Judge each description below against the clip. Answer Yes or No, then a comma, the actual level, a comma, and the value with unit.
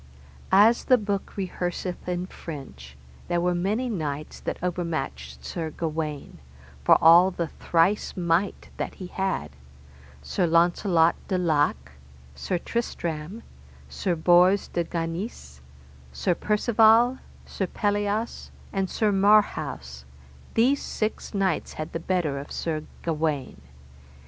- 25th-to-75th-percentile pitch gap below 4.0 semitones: No, average, 4.3 semitones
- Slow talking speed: Yes, slow, 120 wpm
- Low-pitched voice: No, medium, 175 Hz